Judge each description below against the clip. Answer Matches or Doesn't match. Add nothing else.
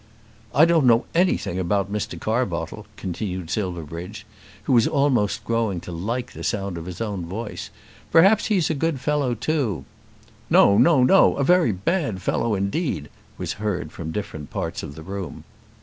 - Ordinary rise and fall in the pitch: Doesn't match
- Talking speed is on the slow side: Doesn't match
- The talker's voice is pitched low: Matches